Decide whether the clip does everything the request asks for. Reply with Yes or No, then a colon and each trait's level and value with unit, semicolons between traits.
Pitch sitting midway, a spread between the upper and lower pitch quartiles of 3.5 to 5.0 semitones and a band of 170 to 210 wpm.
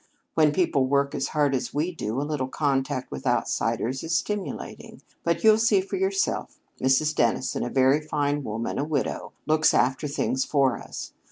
No: medium, 145 Hz; average, 3.1 semitones; average, 175 wpm